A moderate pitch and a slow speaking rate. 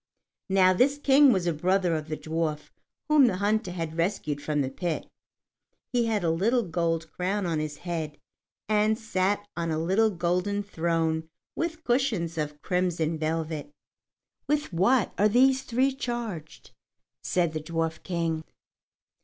No: medium, 180 Hz; average, 150 wpm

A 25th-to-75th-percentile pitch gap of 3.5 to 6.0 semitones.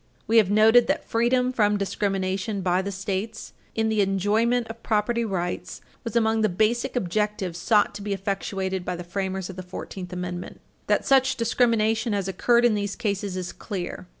No: average, 3.1 semitones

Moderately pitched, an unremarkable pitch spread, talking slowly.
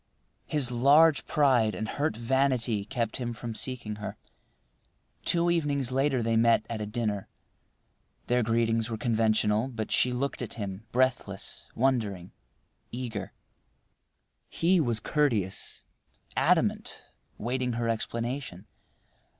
No: low, 120 Hz; average, 3.1 semitones; slow, 120 wpm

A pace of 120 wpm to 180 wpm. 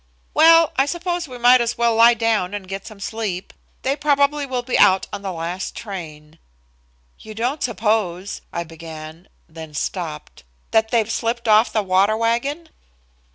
Yes: average, 160 wpm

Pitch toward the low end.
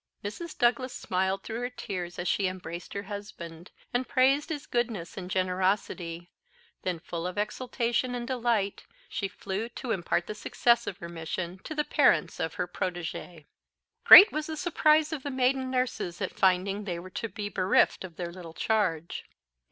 No: high, 200 Hz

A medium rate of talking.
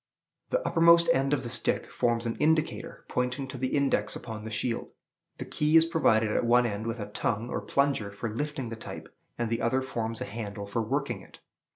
No: fast, 210 wpm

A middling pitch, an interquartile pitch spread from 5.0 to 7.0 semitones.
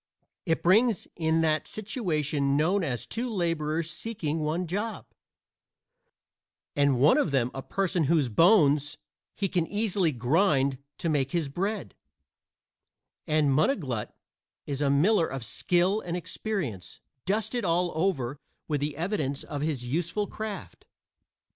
Yes: medium, 160 Hz; wide, 5.4 semitones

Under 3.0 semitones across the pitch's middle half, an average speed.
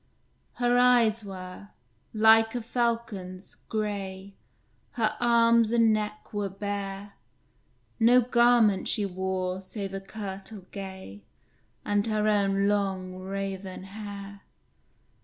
No: narrow, 2.5 semitones; slow, 105 wpm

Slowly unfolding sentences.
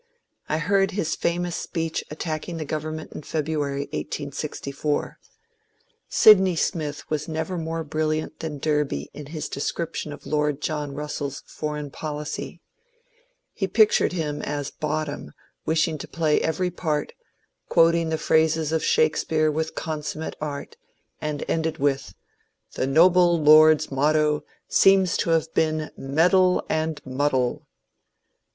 Yes: slow, 130 wpm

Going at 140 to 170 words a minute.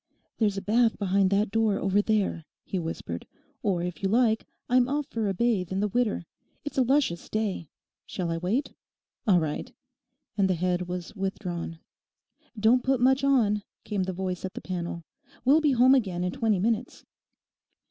No: average, 180 wpm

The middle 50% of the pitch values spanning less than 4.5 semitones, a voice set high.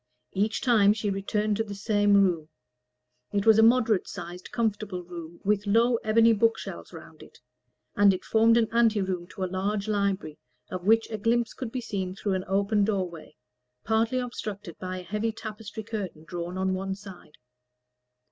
Yes: average, 3.0 semitones; high, 205 Hz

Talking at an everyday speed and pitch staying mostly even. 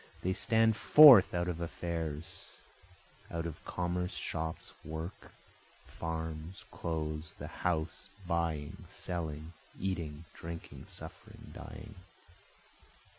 No: slow, 95 wpm; narrow, 2.1 semitones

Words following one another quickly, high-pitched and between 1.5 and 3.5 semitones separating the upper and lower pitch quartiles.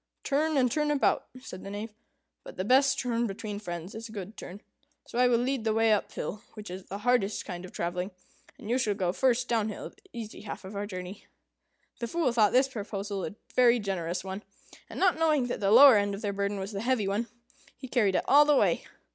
No: fast, 230 wpm; high, 215 Hz; average, 4.0 semitones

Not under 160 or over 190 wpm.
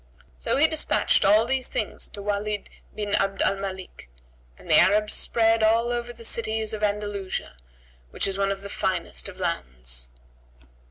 Yes: average, 165 wpm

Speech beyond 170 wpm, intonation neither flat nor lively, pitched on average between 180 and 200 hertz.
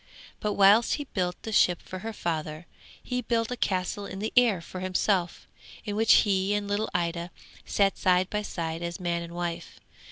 Yes: average, 190 wpm; average, 3.3 semitones; high, 190 Hz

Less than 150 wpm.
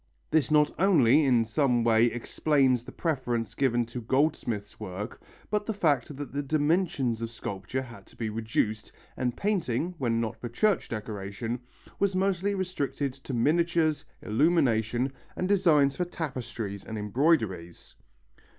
Yes: average, 140 wpm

